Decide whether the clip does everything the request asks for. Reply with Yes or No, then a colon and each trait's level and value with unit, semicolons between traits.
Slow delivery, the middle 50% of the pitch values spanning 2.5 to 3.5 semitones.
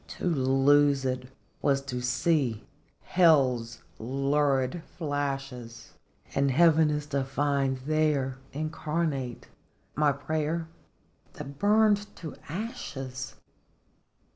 Yes: slow, 90 wpm; average, 2.8 semitones